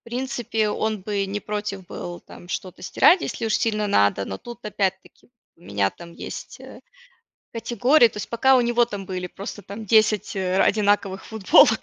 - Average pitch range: Yes, average, 3.1 semitones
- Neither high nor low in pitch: No, high, 210 Hz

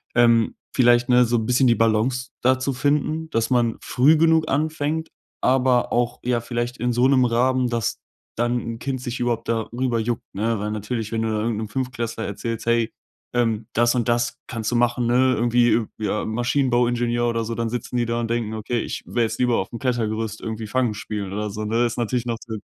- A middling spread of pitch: No, narrow, 1.7 semitones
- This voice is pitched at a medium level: No, low, 120 Hz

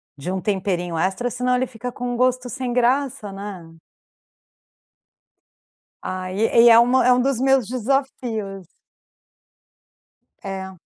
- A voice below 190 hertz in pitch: No, high, 235 Hz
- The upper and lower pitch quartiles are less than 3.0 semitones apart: No, average, 4.6 semitones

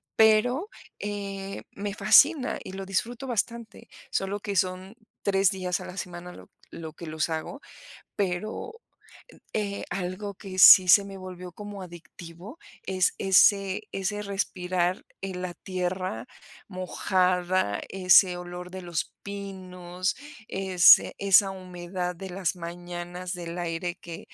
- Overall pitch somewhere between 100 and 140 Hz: No, medium, 185 Hz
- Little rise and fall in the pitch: Yes, narrow, 2.0 semitones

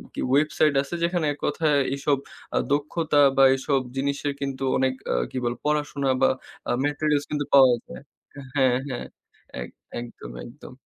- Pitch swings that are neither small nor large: No, narrow, 2.0 semitones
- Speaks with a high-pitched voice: No, medium, 140 Hz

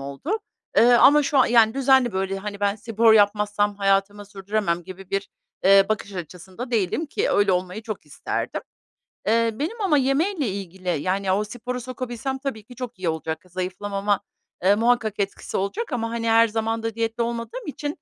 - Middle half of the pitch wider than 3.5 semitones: Yes, average, 4.0 semitones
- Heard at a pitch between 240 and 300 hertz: No, high, 215 Hz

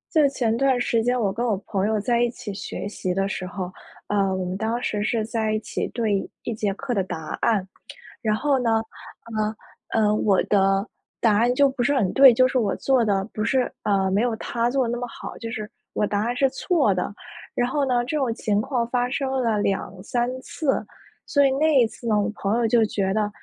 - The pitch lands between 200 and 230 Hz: Yes, high, 225 Hz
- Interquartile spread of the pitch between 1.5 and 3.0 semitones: No, average, 3.5 semitones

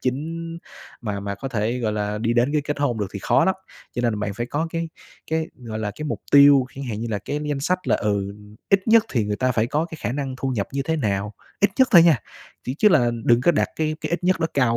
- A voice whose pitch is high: No, low, 130 Hz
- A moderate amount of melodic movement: No, wide, 6.2 semitones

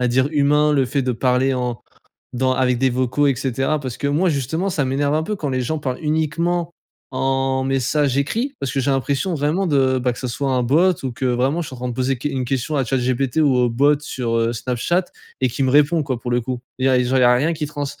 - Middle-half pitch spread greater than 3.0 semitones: No, average, 2.7 semitones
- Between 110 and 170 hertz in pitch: Yes, low, 135 Hz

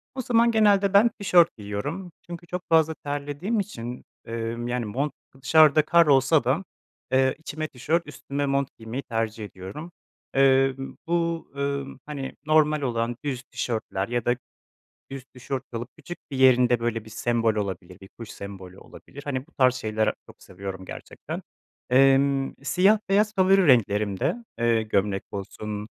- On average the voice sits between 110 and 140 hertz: Yes, low, 135 Hz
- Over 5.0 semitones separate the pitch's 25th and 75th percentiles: Yes, wide, 5.6 semitones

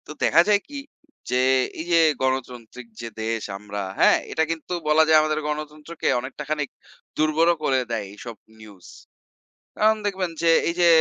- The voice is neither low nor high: Yes, medium, 150 Hz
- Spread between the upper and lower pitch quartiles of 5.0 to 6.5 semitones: Yes, wide, 5.5 semitones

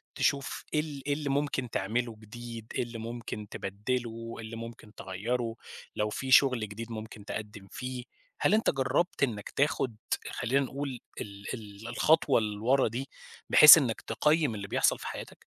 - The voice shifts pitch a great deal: No, average, 3.8 semitones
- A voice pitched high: No, low, 120 Hz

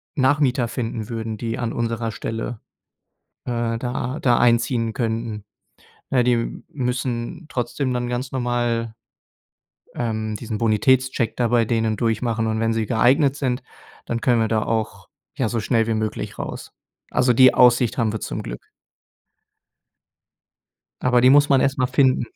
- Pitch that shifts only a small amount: Yes, narrow, 2.0 semitones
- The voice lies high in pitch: No, low, 120 Hz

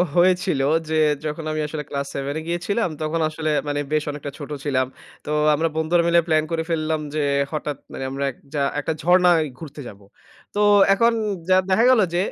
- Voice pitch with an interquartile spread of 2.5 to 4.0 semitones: Yes, average, 2.9 semitones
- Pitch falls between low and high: Yes, medium, 155 Hz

